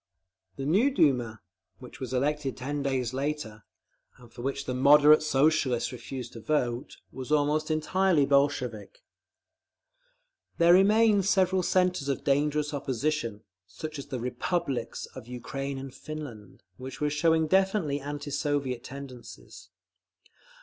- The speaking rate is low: Yes, slow, 130 wpm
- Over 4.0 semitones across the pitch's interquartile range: No, average, 3.3 semitones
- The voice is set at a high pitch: No, medium, 140 Hz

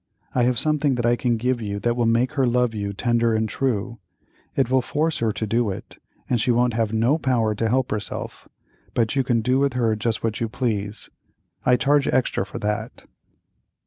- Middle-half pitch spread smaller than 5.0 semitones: Yes, narrow, 2.5 semitones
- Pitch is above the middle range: No, low, 120 Hz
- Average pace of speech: No, fast, 210 wpm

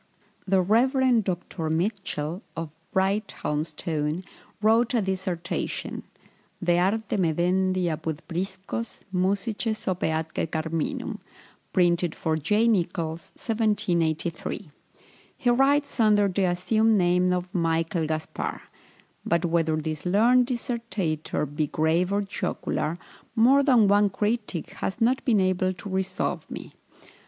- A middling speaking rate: No, slow, 115 wpm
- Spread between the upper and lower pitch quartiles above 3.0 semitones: Yes, average, 4.6 semitones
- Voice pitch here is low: No, medium, 185 Hz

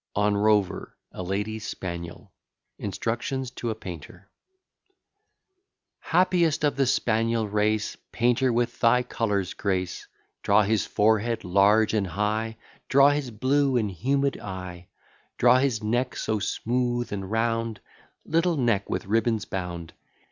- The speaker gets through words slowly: Yes, slow, 125 wpm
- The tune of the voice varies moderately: Yes, average, 3.5 semitones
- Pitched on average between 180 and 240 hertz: No, low, 110 Hz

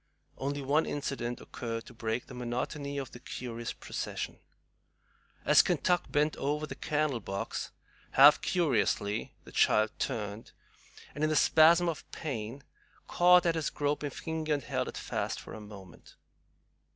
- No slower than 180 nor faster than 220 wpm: No, average, 150 wpm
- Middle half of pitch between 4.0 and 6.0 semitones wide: Yes, average, 4.8 semitones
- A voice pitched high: No, medium, 140 Hz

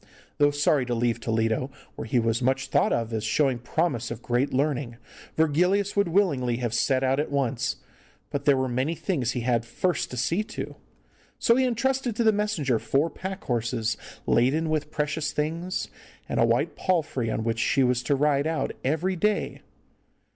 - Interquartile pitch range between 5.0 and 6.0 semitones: Yes, average, 5.3 semitones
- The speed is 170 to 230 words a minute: Yes, average, 185 wpm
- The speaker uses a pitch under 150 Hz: Yes, medium, 140 Hz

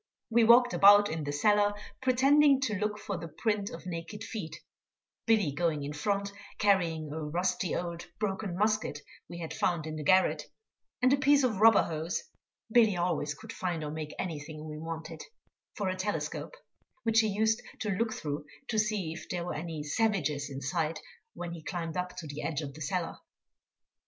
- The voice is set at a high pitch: No, medium, 180 Hz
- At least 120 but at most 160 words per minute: No, average, 185 wpm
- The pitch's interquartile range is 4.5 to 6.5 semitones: Yes, average, 5.2 semitones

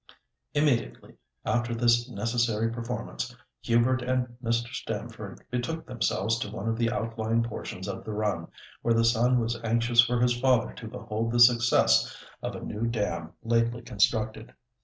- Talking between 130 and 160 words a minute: Yes, average, 155 wpm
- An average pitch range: No, narrow, 1.2 semitones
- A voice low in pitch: Yes, low, 115 Hz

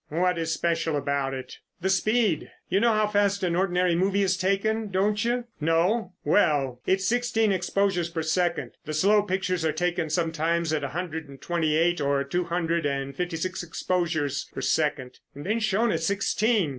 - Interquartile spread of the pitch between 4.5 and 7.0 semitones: No, average, 3.8 semitones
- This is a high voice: No, medium, 175 Hz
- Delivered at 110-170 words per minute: No, average, 180 wpm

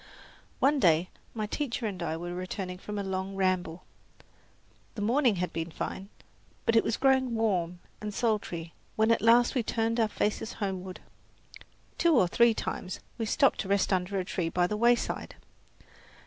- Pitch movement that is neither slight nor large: Yes, average, 4.0 semitones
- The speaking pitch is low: No, high, 205 Hz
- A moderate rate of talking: Yes, average, 170 wpm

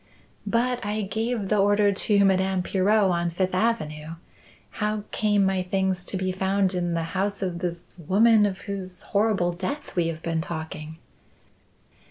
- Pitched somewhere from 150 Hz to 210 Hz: Yes, high, 190 Hz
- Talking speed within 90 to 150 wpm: No, average, 160 wpm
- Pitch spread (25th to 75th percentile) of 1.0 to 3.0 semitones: Yes, average, 2.7 semitones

